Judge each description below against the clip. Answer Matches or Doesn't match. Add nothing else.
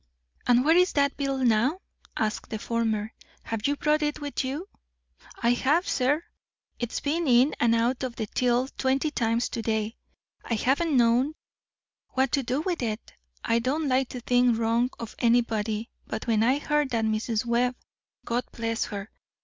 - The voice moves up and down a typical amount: Matches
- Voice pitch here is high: Matches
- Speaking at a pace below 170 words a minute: Doesn't match